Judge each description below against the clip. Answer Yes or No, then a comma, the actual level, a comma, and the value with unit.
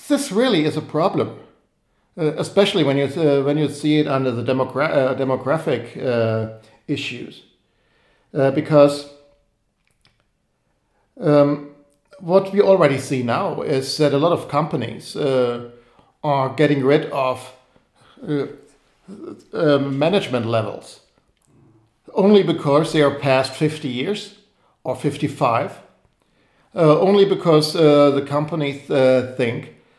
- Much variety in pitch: No, average, 2.8 semitones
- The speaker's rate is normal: No, slow, 120 wpm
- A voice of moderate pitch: Yes, medium, 145 Hz